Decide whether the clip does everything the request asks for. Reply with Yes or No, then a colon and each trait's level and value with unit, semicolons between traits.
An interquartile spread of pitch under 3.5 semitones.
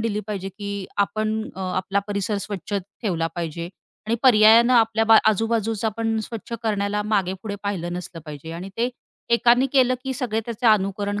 Yes: average, 2.8 semitones